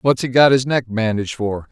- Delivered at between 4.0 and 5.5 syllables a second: Yes, 5.4 syllables/s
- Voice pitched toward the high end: No, low, 120 Hz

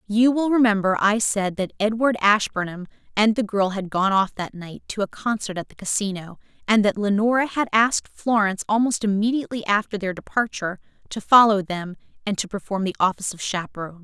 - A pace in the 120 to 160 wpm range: No, average, 185 wpm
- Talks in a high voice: Yes, high, 205 Hz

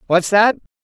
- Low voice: No, high, 210 Hz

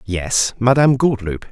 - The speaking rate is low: Yes, slow, 120 wpm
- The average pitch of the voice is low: Yes, low, 110 Hz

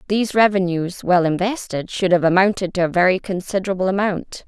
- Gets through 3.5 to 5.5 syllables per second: No, 5.9 syllables/s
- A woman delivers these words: Yes, female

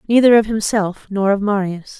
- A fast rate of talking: No, average, 180 wpm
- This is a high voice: Yes, high, 205 Hz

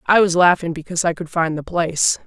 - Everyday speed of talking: No, fast, 240 wpm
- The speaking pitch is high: No, medium, 170 Hz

